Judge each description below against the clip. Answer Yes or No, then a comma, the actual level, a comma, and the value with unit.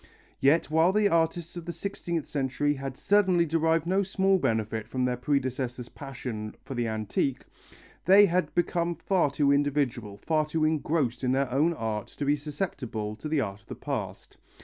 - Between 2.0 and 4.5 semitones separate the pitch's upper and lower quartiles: No, average, 5.1 semitones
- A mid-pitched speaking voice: Yes, medium, 145 Hz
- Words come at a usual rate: Yes, average, 175 wpm